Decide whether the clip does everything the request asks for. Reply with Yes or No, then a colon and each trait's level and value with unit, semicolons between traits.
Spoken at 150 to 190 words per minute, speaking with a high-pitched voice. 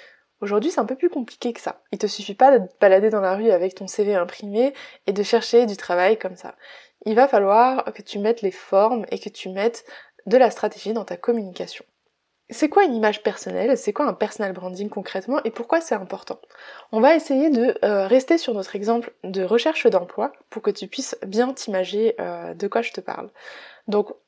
No: average, 215 wpm; high, 215 Hz